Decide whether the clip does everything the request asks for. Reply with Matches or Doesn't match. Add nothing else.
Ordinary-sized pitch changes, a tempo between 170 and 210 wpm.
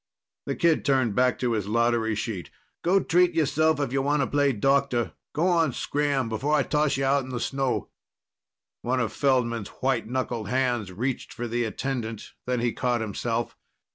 Matches